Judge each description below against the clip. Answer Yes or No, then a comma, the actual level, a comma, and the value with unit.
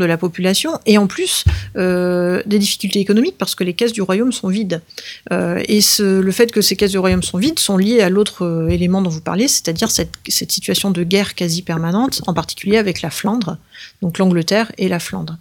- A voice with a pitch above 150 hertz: Yes, high, 190 Hz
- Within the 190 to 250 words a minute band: Yes, fast, 220 wpm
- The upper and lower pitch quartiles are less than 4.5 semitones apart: Yes, average, 2.9 semitones